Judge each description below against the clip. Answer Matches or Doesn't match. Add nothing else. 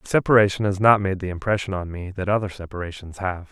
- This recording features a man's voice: Matches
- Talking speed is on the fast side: Matches